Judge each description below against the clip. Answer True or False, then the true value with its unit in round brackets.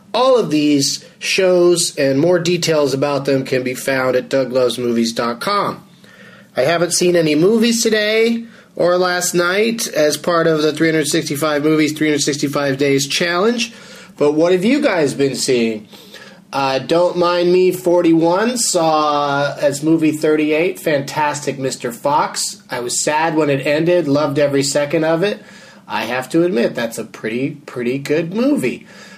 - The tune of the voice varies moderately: True (4.0 semitones)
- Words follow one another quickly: False (150 wpm)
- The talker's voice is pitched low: False (155 Hz)